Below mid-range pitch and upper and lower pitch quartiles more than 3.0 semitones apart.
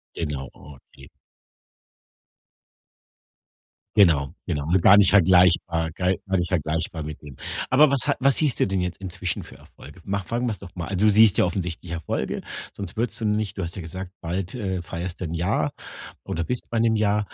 Yes: very low, 90 Hz; average, 3.8 semitones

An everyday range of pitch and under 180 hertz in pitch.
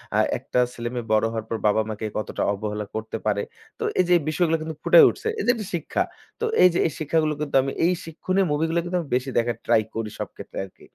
No: wide, 7.5 semitones; medium, 140 Hz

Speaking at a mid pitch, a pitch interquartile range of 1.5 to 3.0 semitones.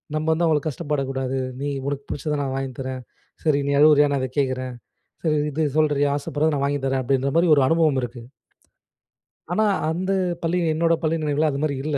Yes: medium, 145 Hz; narrow, 2.5 semitones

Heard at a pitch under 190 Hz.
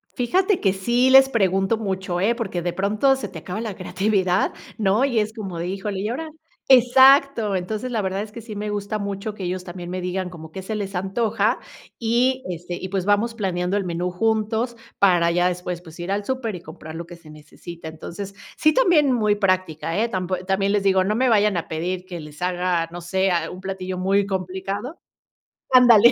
No: high, 195 Hz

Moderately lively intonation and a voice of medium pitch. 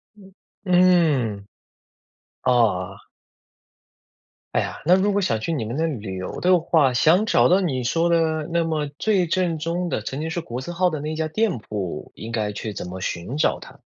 No: wide, 7.4 semitones; medium, 155 Hz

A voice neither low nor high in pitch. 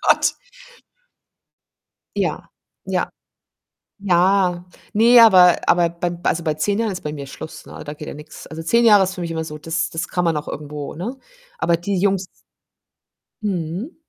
Yes: medium, 175 Hz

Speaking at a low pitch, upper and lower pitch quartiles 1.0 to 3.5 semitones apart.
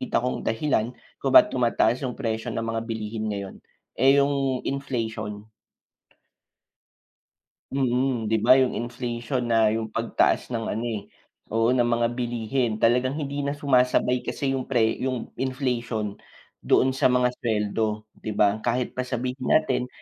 Yes: low, 120 Hz; narrow, 2.5 semitones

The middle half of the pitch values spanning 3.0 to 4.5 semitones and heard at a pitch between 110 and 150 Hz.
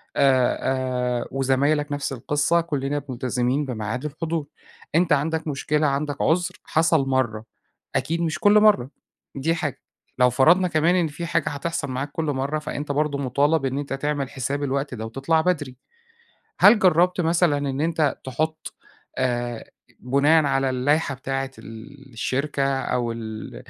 Yes: average, 3.3 semitones; medium, 140 Hz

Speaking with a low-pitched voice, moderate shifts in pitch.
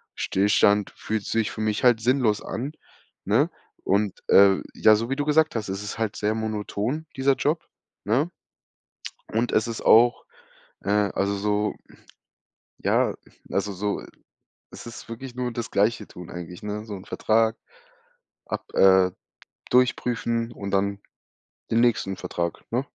Yes: low, 110 Hz; average, 3.0 semitones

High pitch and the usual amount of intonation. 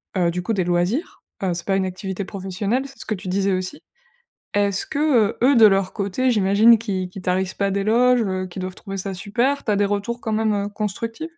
Yes: high, 200 Hz; average, 3.3 semitones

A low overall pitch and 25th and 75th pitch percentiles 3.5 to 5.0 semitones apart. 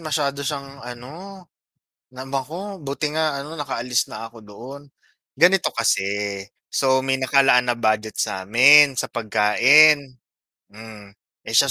Yes: low, 130 Hz; average, 4.4 semitones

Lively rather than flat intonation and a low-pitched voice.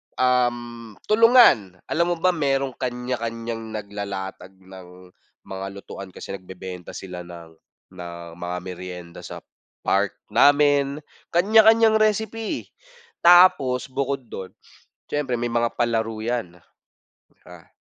Yes: wide, 7.0 semitones; low, 115 Hz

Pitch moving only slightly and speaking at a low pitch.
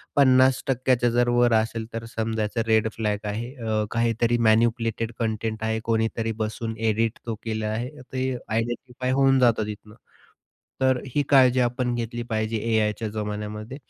Yes: narrow, 1.8 semitones; low, 115 Hz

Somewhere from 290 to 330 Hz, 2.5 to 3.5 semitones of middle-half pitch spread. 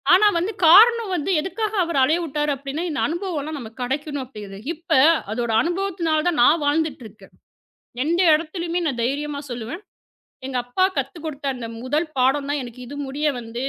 No: very high, 295 Hz; average, 4.7 semitones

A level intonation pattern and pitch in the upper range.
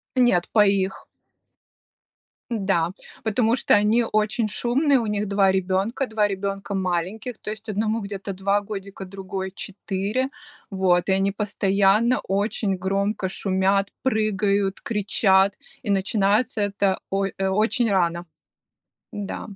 Yes: narrow, 2.0 semitones; high, 200 Hz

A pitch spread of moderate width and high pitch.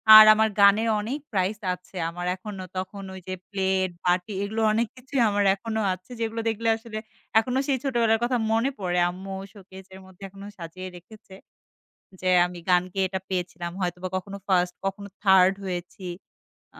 Yes: average, 3.1 semitones; high, 195 Hz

